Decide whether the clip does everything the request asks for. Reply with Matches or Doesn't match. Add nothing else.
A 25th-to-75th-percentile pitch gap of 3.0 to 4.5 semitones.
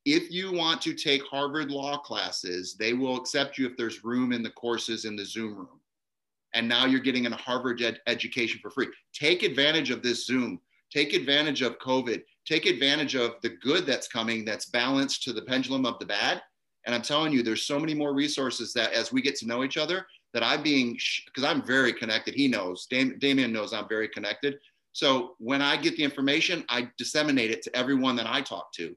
Matches